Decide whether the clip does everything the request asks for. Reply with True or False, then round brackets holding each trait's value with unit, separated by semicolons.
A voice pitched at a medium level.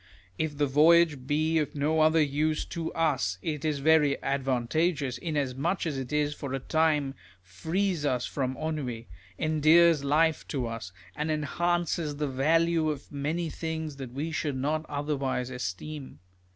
True (150 Hz)